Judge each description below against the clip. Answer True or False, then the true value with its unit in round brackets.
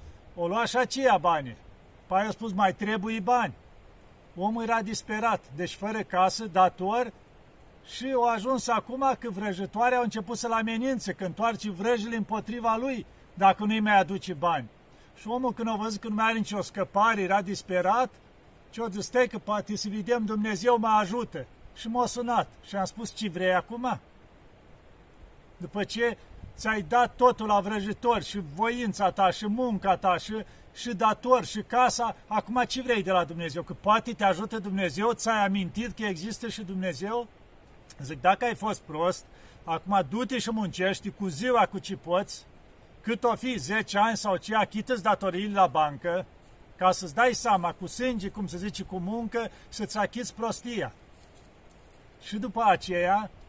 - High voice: True (210 Hz)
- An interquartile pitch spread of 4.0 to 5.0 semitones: False (3.5 semitones)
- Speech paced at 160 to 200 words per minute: True (165 wpm)